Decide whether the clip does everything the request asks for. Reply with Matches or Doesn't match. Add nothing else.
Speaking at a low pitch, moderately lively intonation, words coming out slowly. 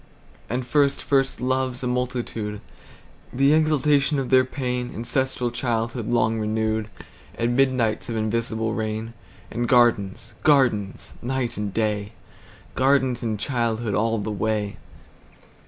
Matches